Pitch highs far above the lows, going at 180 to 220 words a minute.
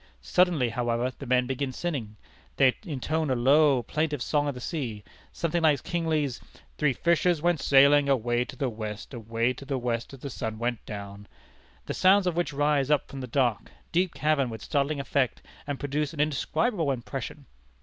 No: average, 4.0 semitones; average, 185 wpm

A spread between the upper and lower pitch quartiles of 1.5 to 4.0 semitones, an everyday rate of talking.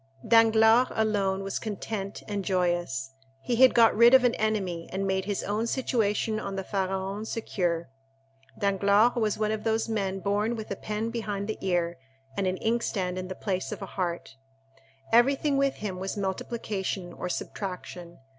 Yes: average, 2.9 semitones; average, 160 wpm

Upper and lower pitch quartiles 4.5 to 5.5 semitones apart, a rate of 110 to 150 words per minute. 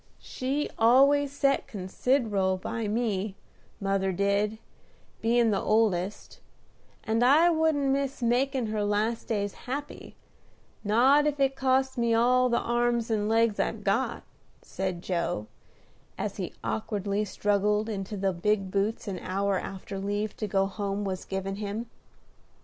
No: average, 3.9 semitones; average, 140 wpm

